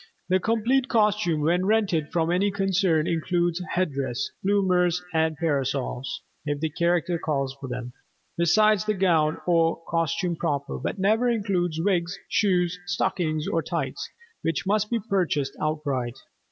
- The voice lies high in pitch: No, medium, 175 Hz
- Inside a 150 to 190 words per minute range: No, average, 140 wpm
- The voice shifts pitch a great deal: No, average, 3.9 semitones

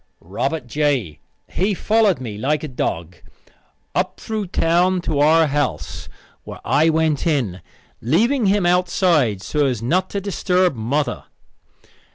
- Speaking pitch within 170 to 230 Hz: No, medium, 155 Hz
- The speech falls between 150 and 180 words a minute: No, slow, 135 wpm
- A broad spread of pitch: Yes, wide, 6.1 semitones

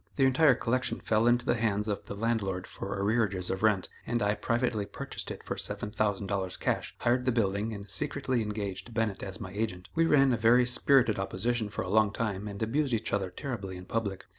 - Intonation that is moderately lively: Yes, average, 3.2 semitones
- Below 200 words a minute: No, fast, 205 wpm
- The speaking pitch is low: Yes, low, 110 Hz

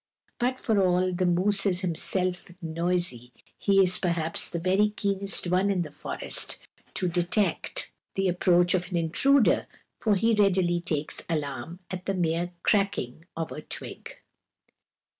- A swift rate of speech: No, average, 145 wpm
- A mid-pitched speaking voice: Yes, medium, 180 Hz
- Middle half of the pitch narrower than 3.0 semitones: Yes, narrow, 2.4 semitones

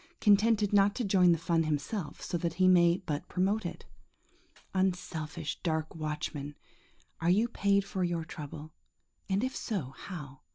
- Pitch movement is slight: No, average, 4.0 semitones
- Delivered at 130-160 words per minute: Yes, average, 155 wpm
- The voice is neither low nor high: Yes, medium, 175 Hz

